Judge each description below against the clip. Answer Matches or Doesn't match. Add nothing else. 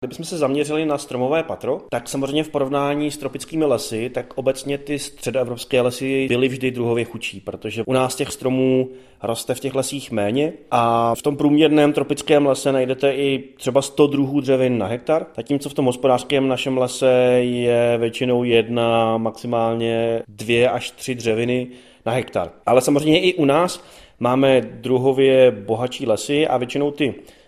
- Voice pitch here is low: Matches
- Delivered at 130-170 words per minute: Matches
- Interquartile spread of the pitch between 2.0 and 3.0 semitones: Matches